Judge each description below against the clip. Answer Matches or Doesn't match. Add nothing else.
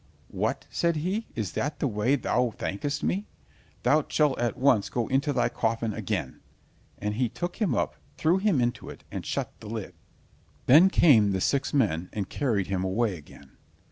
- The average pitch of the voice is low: Matches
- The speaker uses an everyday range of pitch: Doesn't match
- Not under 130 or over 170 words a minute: Doesn't match